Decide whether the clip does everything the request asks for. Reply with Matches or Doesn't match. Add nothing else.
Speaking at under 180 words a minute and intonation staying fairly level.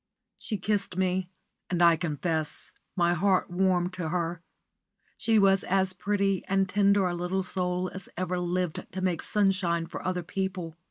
Matches